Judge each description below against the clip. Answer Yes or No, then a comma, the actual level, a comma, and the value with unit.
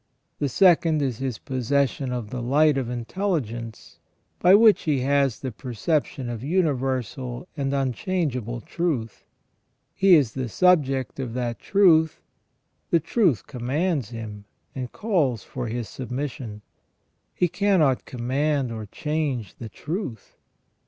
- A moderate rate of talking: No, slow, 130 wpm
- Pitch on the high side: No, low, 135 Hz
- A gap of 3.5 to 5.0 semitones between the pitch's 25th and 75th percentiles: Yes, average, 4.7 semitones